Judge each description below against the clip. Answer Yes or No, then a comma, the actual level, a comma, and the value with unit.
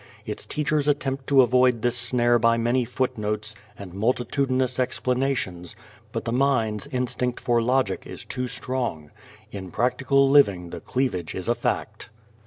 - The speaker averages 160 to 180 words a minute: No, average, 145 wpm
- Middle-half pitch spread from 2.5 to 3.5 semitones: Yes, average, 3.2 semitones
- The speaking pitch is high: No, low, 125 Hz